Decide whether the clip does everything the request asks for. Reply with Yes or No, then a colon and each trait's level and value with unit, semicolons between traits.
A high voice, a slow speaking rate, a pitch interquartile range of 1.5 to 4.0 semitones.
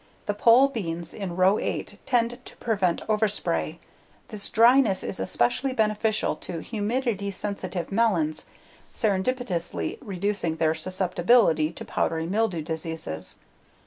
No: high, 200 Hz; slow, 115 wpm; average, 5.1 semitones